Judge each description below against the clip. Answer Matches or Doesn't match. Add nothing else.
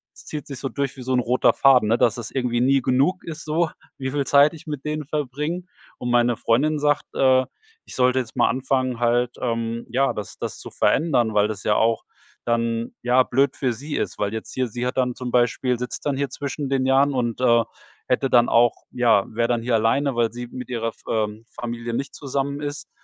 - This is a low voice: Matches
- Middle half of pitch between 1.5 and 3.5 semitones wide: Matches